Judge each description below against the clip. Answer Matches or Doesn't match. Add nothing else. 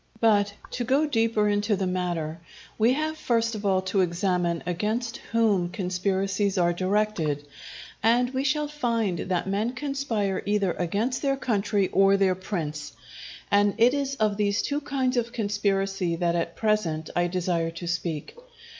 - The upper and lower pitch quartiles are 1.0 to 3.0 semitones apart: Doesn't match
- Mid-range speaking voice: Doesn't match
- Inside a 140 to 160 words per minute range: Matches